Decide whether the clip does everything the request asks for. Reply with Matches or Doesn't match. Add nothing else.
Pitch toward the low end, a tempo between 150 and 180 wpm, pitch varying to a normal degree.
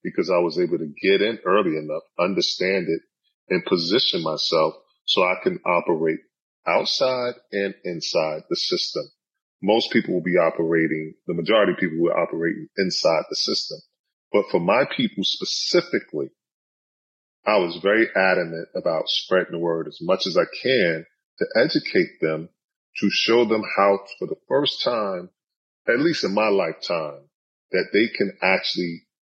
Doesn't match